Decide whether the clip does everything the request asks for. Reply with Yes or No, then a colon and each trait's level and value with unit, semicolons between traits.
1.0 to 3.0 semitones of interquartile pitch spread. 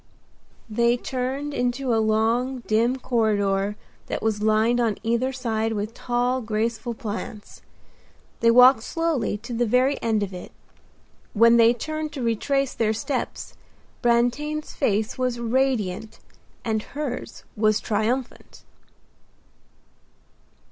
Yes: average, 2.7 semitones